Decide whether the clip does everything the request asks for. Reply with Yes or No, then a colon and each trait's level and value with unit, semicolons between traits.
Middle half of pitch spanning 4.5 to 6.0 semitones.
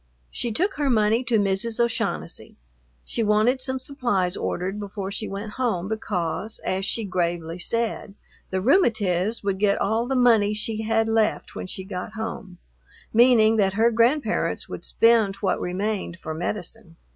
No: average, 3.2 semitones